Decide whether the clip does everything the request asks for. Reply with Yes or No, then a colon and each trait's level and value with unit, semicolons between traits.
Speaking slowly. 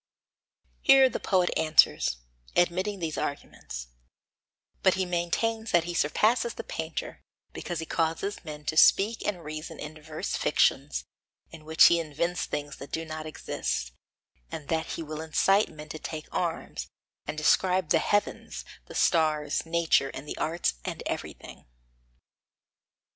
No: average, 145 wpm